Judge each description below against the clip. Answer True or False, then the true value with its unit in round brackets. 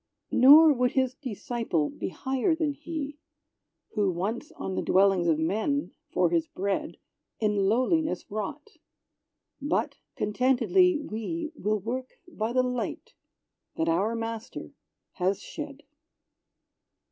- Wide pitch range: True (6.3 semitones)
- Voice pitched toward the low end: False (245 Hz)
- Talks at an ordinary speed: False (120 wpm)